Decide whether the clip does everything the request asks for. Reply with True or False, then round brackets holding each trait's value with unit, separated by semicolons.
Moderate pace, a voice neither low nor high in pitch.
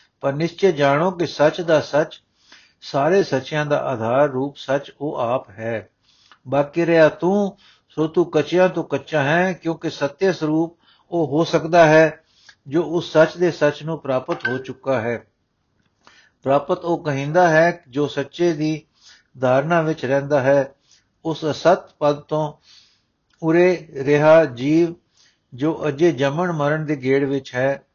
True (145 wpm; 155 Hz)